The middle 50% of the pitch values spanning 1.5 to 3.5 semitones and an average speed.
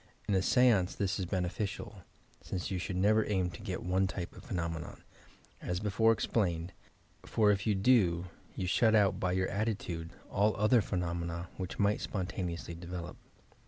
Yes: average, 2.9 semitones; average, 175 wpm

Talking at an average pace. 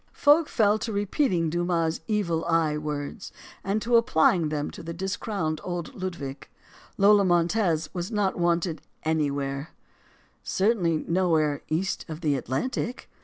No: slow, 125 wpm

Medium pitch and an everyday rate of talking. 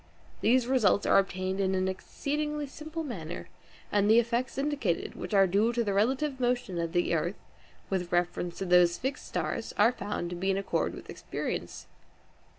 No: high, 205 Hz; average, 175 wpm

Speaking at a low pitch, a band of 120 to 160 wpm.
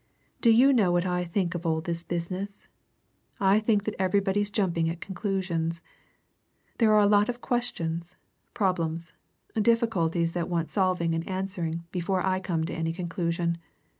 No: medium, 180 Hz; average, 150 wpm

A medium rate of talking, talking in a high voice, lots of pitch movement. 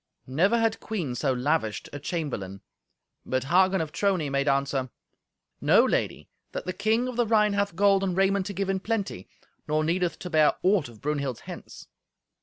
No: average, 180 wpm; medium, 175 Hz; wide, 6.1 semitones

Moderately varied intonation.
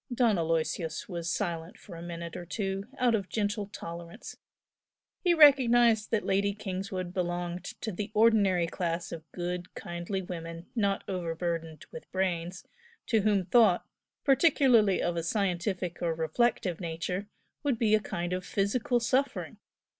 Yes: average, 3.9 semitones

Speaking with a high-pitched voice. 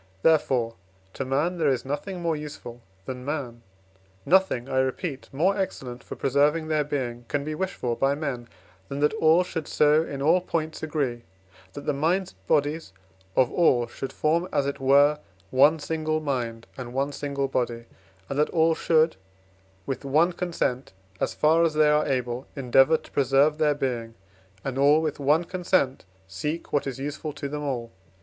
No: medium, 145 Hz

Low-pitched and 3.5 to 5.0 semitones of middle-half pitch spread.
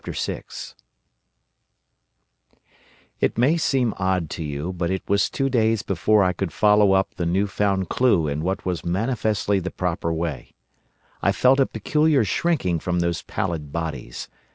Yes: very low, 95 Hz; average, 4.5 semitones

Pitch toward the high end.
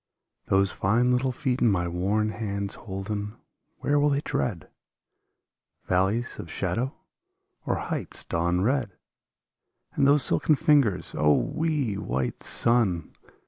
No: low, 110 Hz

